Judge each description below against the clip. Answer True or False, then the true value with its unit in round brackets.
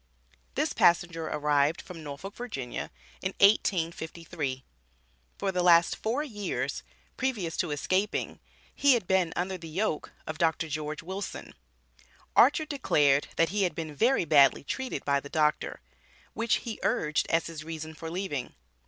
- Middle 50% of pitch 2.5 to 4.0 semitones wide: False (4.5 semitones)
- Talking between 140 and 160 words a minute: True (145 wpm)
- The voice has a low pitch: False (165 Hz)